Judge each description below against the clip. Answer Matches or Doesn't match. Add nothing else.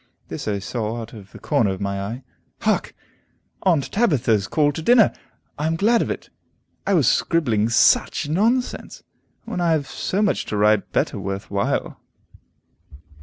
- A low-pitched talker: Matches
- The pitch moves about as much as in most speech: Doesn't match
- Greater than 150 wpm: Matches